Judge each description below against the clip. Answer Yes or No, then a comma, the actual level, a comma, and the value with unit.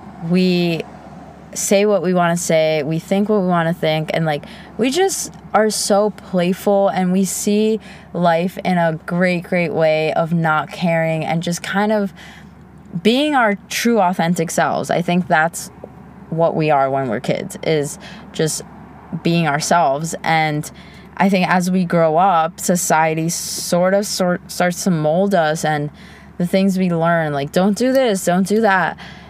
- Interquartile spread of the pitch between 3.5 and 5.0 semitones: No, average, 3.1 semitones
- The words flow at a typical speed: Yes, average, 170 wpm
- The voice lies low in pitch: No, medium, 180 Hz